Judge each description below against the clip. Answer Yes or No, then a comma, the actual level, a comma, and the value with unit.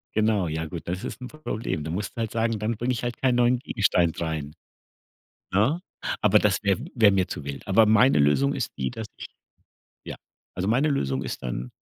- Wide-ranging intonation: Yes, wide, 6.6 semitones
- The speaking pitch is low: Yes, low, 105 Hz